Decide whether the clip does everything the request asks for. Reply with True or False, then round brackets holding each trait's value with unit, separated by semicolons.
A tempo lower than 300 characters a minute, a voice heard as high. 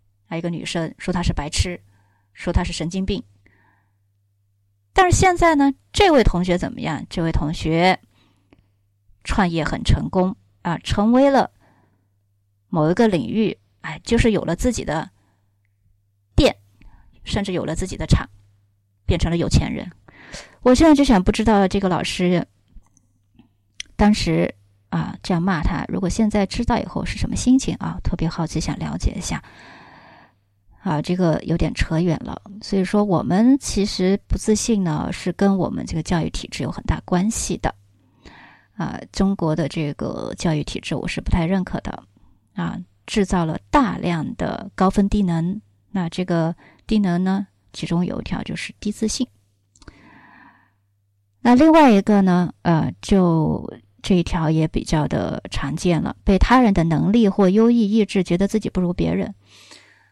False (230 characters per minute; 170 Hz)